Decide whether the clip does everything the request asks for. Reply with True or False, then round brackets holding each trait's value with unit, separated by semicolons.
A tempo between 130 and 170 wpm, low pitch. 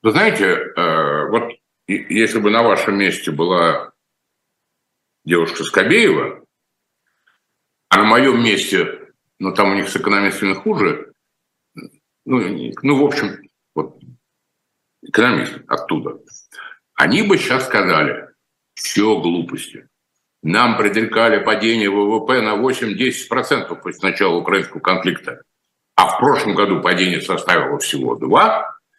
False (110 wpm; 110 Hz)